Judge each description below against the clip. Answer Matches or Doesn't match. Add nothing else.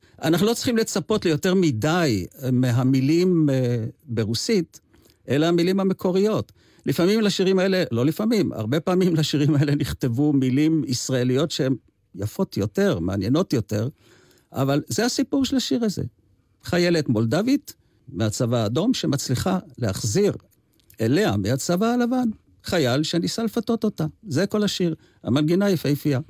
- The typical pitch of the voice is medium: Matches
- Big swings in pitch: Matches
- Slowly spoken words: Doesn't match